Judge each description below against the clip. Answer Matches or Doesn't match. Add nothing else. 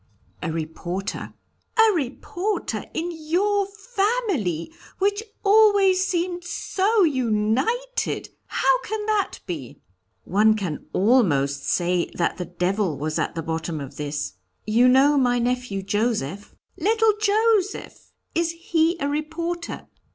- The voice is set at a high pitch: Matches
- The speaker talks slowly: Matches